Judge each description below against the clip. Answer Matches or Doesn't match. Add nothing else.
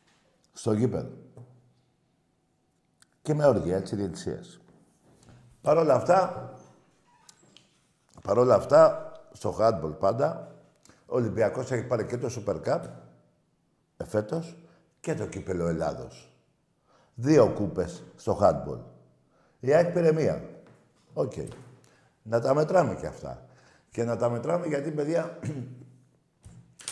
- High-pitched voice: Doesn't match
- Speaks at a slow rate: Matches